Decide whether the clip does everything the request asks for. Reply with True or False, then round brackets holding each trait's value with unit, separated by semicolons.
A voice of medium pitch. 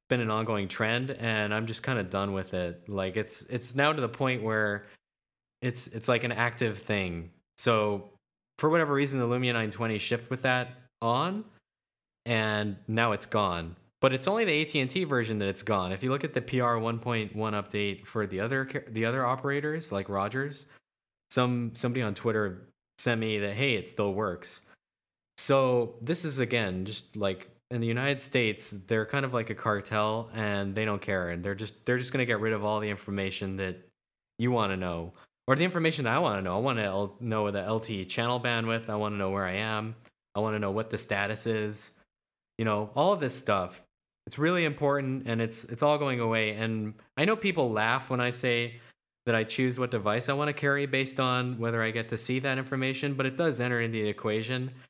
False (115 Hz)